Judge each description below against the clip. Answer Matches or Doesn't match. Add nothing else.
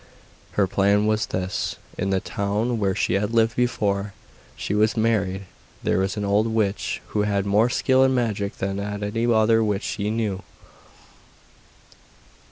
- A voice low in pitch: Matches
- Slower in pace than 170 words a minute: Matches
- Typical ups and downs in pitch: Doesn't match